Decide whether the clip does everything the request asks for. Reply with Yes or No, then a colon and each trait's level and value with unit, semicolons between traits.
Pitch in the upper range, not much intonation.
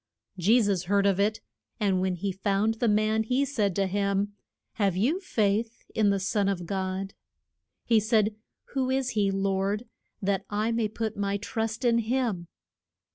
Yes: high, 205 Hz; narrow, 2.3 semitones